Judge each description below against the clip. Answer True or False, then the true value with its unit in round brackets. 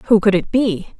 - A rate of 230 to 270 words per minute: True (240 wpm)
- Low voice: False (205 Hz)